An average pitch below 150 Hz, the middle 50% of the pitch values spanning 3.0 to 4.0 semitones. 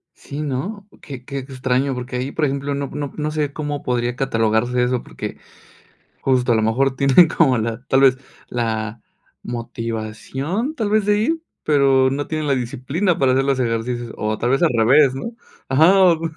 Yes: low, 135 Hz; average, 3.5 semitones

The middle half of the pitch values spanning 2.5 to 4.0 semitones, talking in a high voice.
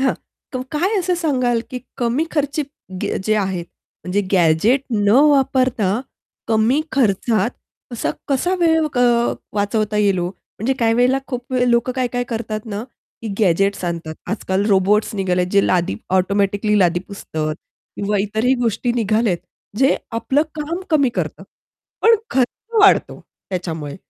No: average, 4.8 semitones; high, 220 Hz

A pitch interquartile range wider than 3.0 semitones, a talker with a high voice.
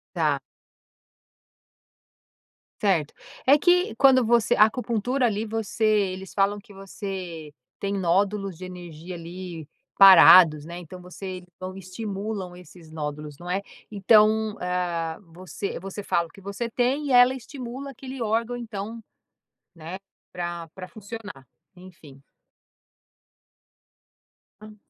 Yes: average, 4.0 semitones; high, 195 Hz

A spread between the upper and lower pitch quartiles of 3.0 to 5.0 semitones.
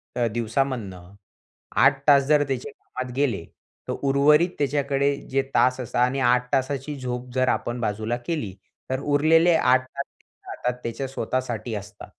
No: narrow, 2.6 semitones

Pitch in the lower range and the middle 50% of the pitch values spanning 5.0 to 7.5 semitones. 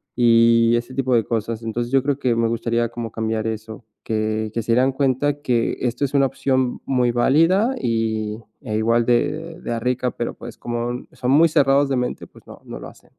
No: low, 120 Hz; narrow, 2.6 semitones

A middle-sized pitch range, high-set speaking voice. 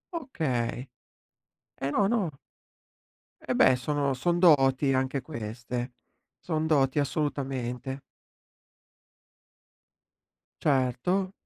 No: average, 3.7 semitones; low, 135 Hz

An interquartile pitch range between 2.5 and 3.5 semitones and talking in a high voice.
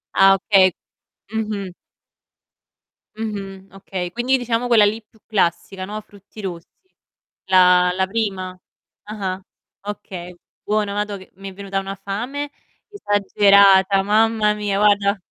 No: narrow, 1.9 semitones; high, 200 Hz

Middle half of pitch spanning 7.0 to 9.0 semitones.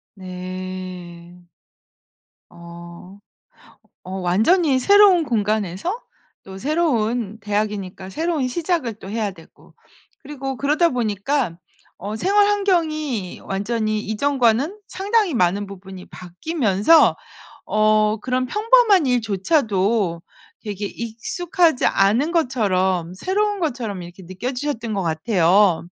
Yes: wide, 7.9 semitones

